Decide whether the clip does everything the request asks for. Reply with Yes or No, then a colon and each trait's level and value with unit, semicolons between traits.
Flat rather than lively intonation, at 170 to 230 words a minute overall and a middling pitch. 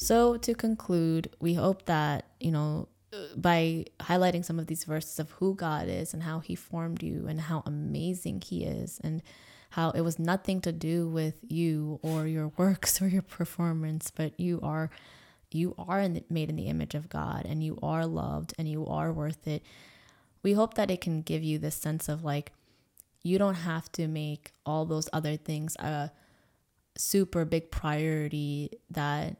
Yes: narrow, 2.1 semitones; average, 185 wpm; medium, 160 Hz